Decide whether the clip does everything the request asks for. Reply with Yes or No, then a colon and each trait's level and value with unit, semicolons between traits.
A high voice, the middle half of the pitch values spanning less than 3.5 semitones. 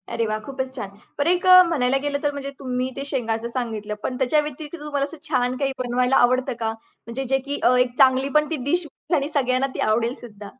Yes: very high, 260 Hz; average, 2.9 semitones